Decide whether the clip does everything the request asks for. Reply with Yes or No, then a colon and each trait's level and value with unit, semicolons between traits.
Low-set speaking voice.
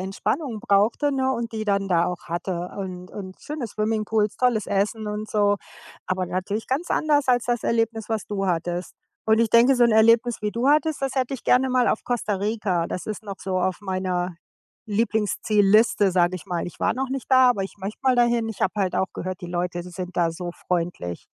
No: high, 210 Hz